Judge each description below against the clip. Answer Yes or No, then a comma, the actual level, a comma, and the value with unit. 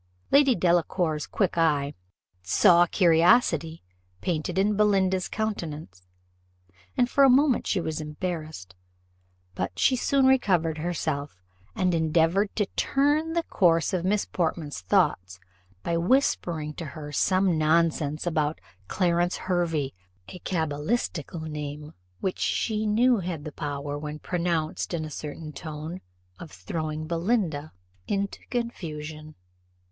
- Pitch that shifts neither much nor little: Yes, average, 4.0 semitones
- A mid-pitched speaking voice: Yes, medium, 165 Hz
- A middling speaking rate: No, slow, 120 wpm